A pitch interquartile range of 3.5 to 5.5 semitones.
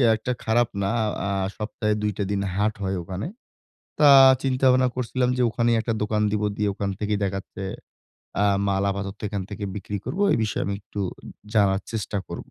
No: average, 2.7 semitones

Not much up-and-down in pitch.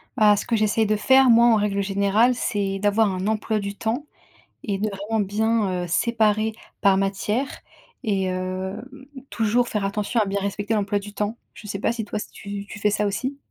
Yes: narrow, 1.9 semitones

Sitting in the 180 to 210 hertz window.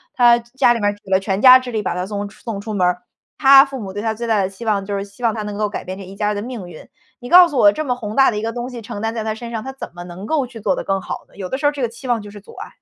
No: high, 220 Hz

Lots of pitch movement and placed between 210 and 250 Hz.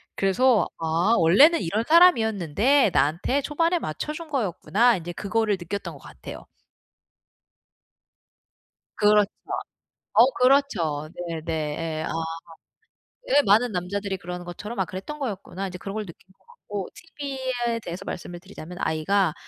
No: wide, 6.4 semitones; high, 200 Hz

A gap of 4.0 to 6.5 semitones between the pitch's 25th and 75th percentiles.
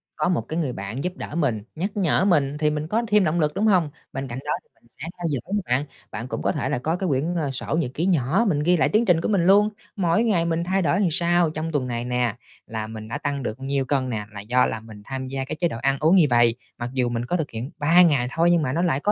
Yes: wide, 5.4 semitones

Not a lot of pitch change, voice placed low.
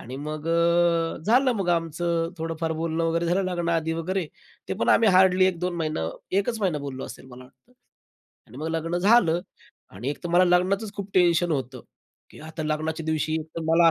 No: narrow, 2.3 semitones; medium, 165 Hz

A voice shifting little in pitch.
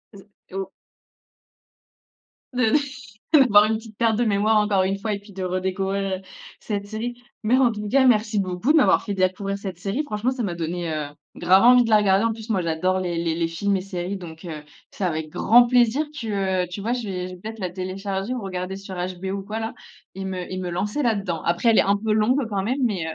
No: average, 3.2 semitones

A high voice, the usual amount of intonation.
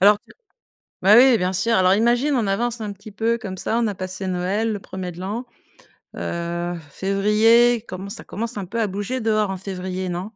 Yes: high, 200 Hz; average, 3.3 semitones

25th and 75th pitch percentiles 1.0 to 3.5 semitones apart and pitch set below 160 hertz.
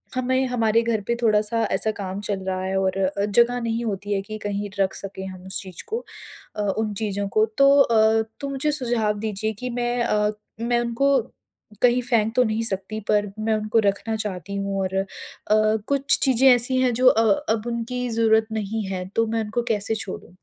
No: average, 3.0 semitones; high, 220 Hz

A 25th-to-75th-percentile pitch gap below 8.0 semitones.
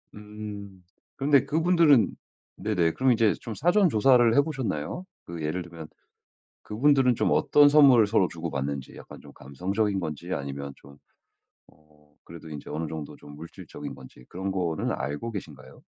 No: wide, 8.5 semitones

